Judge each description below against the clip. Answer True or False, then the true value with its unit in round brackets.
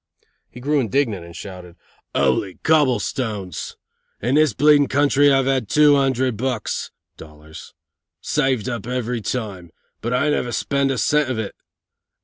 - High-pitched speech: False (125 Hz)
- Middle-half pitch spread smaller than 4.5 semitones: False (5.2 semitones)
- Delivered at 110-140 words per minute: True (135 wpm)